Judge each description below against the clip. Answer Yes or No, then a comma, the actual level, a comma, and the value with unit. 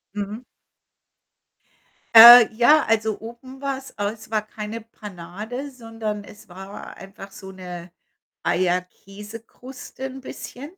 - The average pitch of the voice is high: Yes, high, 220 Hz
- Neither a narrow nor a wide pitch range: Yes, average, 3.8 semitones